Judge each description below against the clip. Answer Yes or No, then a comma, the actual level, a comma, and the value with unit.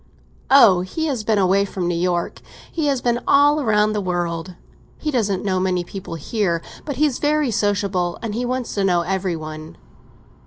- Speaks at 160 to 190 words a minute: Yes, average, 180 wpm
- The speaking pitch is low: No, high, 200 Hz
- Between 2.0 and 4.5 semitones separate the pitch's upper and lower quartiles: No, wide, 5.5 semitones